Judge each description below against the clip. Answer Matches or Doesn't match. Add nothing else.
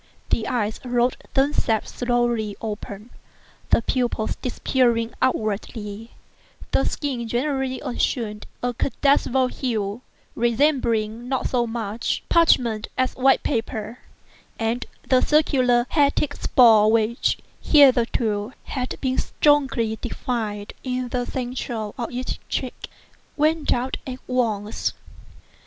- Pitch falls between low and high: Doesn't match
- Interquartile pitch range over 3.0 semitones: Doesn't match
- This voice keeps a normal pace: Doesn't match